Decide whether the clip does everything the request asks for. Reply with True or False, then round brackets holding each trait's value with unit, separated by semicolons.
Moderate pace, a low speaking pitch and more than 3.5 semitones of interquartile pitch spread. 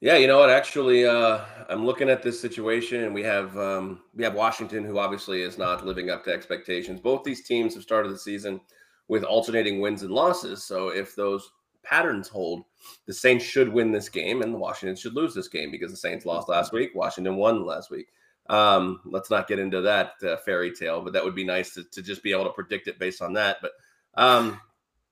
False (220 wpm; 105 Hz; 3.9 semitones)